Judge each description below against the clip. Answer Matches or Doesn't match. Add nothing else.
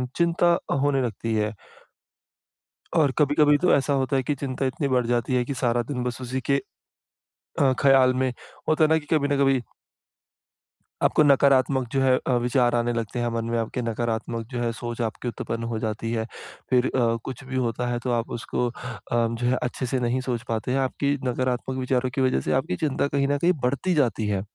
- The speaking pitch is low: Matches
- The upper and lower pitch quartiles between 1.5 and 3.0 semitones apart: Matches